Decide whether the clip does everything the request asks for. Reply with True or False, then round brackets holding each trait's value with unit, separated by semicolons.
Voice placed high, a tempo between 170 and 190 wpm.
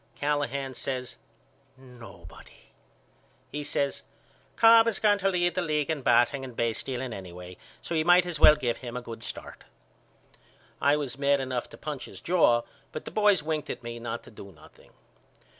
False (140 Hz; 175 wpm)